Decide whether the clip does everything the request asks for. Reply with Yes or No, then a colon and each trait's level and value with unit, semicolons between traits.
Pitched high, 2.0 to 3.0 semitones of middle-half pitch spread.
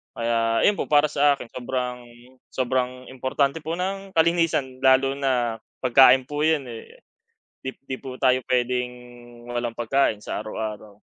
No: low, 130 Hz; narrow, 2.6 semitones